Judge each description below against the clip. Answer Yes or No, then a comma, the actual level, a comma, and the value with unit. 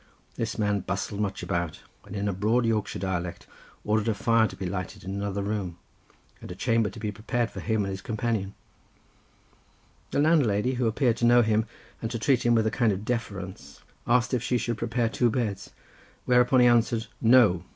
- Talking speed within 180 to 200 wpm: Yes, average, 195 wpm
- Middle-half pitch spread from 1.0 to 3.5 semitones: Yes, average, 3.0 semitones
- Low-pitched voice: Yes, low, 110 Hz